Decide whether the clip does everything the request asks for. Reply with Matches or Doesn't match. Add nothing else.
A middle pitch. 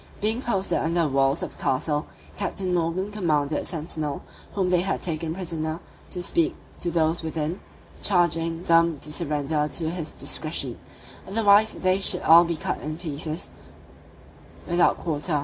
Matches